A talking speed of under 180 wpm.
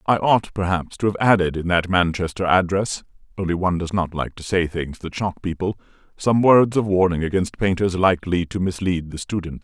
No: average, 200 wpm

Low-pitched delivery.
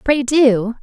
No: very high, 250 Hz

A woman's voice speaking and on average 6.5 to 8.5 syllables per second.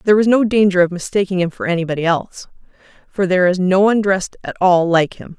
Yes: female; 6.8 syllables/s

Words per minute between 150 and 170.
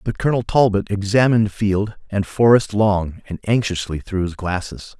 Yes: average, 155 wpm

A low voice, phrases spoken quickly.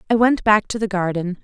No: high, 205 Hz; fast, 250 wpm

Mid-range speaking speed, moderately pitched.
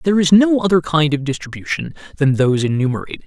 Yes: average, 185 wpm; medium, 155 Hz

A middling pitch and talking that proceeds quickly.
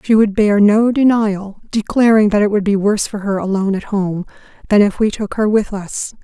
No: high, 205 Hz; fast, 220 wpm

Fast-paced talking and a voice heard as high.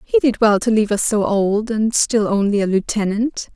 Yes: fast, 220 wpm; high, 215 Hz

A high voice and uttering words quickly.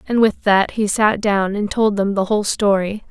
Yes: high, 205 Hz; fast, 230 wpm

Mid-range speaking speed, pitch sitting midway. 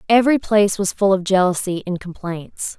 No: average, 170 wpm; high, 195 Hz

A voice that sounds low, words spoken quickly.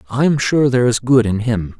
Yes: low, 120 Hz; fast, 265 wpm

